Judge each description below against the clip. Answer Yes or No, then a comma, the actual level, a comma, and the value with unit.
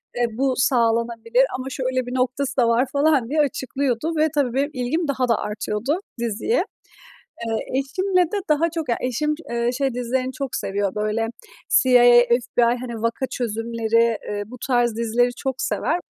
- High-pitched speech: Yes, very high, 250 Hz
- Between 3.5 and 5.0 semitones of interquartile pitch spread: No, average, 3.0 semitones